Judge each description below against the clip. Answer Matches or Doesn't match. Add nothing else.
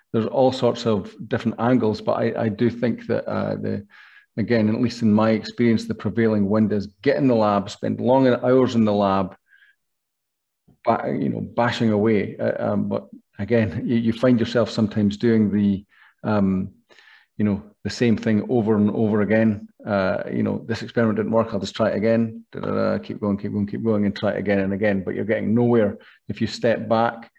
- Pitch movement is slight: Matches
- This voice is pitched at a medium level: Doesn't match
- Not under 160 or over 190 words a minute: Doesn't match